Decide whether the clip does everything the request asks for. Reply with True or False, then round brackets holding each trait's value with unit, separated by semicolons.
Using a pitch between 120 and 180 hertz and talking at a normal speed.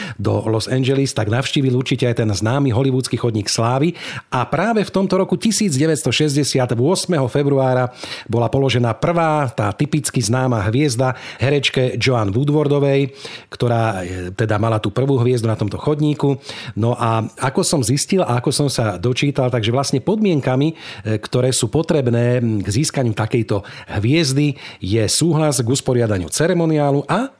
True (130 Hz; 140 wpm)